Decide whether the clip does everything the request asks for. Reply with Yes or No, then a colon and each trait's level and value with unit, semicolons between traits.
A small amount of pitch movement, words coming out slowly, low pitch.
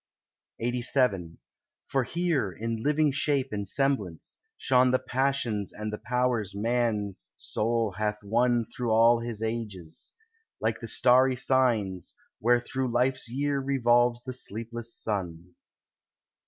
No: average, 3.3 semitones; slow, 125 wpm; low, 120 Hz